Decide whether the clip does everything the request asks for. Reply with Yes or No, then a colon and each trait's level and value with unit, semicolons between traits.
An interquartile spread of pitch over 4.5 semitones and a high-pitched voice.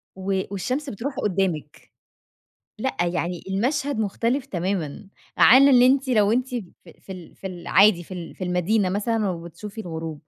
Yes: average, 5.0 semitones; high, 200 Hz